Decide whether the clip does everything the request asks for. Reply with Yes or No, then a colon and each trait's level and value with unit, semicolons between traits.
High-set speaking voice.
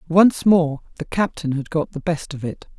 No: medium, 165 Hz